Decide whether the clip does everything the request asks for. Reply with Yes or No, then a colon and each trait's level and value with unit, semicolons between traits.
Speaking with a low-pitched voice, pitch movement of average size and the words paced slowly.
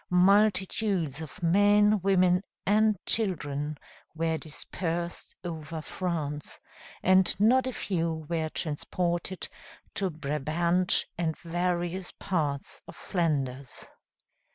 No: medium, 175 Hz; average, 3.2 semitones; slow, 95 wpm